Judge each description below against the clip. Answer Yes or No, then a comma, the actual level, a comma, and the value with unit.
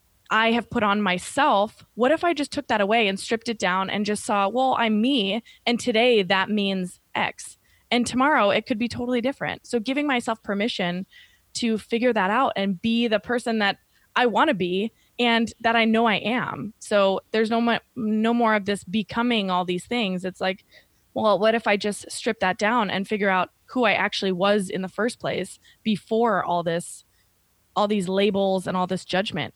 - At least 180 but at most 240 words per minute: Yes, average, 200 wpm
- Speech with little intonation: No, average, 3.4 semitones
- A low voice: No, high, 210 Hz